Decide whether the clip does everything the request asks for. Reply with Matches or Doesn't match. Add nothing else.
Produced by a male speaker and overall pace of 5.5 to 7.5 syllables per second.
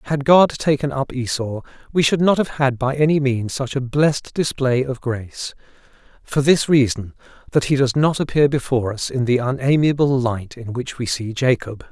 Doesn't match